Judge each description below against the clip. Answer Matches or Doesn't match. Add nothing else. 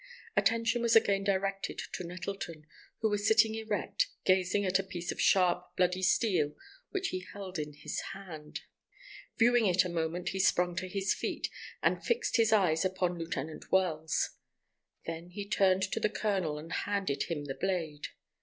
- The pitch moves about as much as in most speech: Matches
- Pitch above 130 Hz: Matches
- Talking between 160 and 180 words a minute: Matches